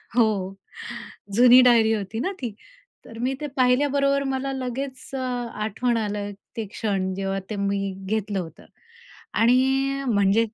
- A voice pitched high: Yes, high, 225 Hz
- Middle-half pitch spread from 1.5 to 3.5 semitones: No, average, 4.0 semitones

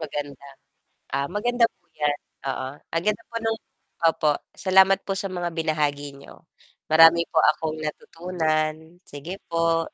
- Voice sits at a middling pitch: Yes, medium, 160 Hz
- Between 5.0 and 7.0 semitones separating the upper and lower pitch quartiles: No, average, 3.2 semitones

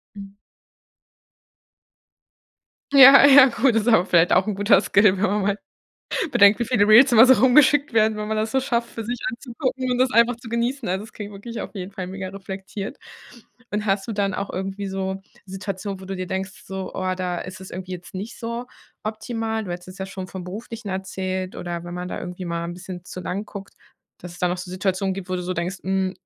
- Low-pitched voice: No, high, 195 Hz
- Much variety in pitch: No, average, 3.3 semitones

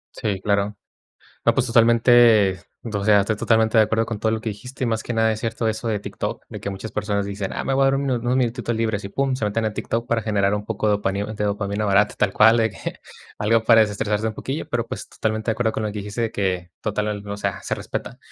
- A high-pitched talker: No, low, 110 Hz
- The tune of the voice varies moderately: No, narrow, 1.9 semitones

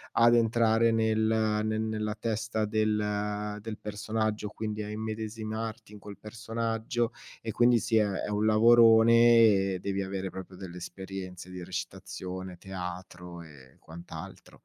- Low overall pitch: Yes, low, 110 Hz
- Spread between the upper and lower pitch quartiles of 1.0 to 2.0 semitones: No, narrow, 2.5 semitones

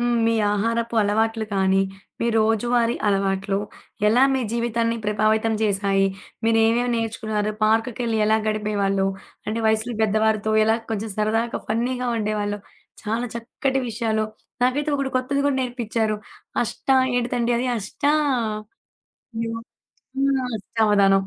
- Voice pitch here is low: No, high, 225 Hz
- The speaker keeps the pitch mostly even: Yes, narrow, 2.0 semitones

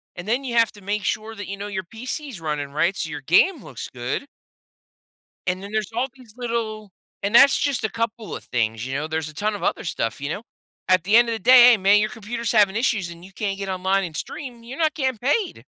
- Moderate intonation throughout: Yes, average, 4.6 semitones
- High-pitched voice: Yes, high, 210 Hz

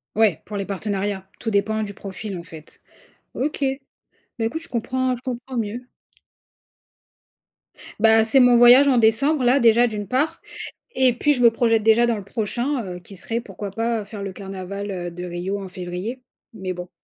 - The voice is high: Yes, high, 220 Hz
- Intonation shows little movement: No, average, 3.9 semitones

